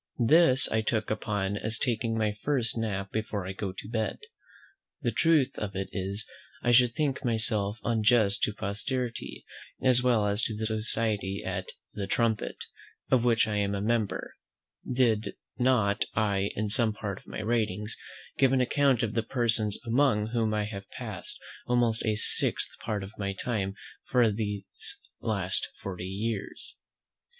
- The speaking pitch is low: Yes, low, 110 Hz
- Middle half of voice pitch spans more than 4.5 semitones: No, average, 2.7 semitones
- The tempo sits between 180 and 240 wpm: No, average, 160 wpm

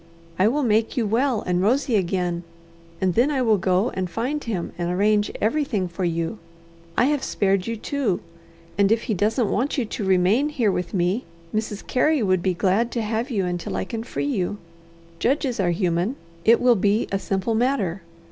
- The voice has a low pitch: No, high, 210 Hz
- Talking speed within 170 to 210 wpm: Yes, average, 195 wpm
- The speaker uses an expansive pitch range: No, average, 4.5 semitones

